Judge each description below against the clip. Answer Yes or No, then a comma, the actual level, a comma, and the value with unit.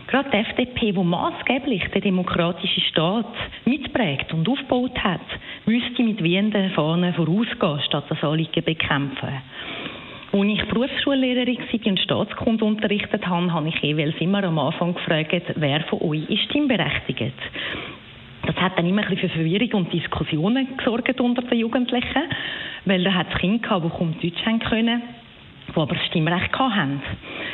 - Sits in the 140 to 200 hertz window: Yes, high, 190 Hz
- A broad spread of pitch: Yes, wide, 5.9 semitones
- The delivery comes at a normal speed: Yes, average, 155 wpm